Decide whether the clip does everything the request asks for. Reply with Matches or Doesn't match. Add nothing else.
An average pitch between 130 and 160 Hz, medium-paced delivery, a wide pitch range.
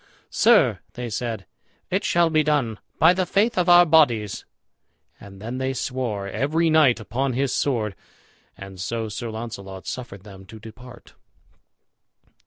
Doesn't match